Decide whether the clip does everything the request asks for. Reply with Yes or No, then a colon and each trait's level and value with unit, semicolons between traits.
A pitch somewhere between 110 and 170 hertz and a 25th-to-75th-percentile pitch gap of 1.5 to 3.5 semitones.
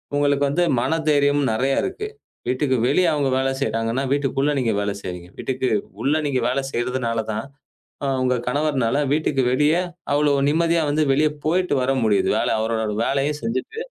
Yes: low, 135 Hz; average, 3.0 semitones